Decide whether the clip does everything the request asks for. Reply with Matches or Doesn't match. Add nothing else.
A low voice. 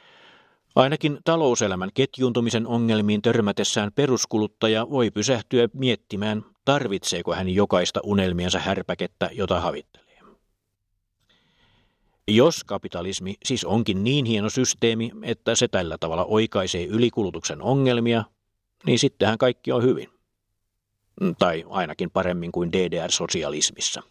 Matches